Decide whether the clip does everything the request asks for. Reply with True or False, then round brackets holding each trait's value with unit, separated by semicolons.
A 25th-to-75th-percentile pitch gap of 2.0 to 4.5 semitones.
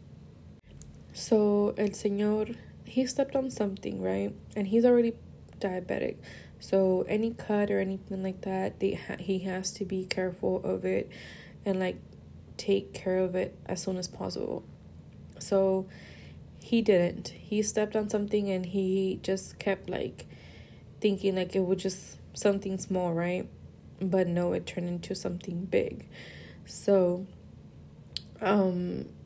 True (2.5 semitones)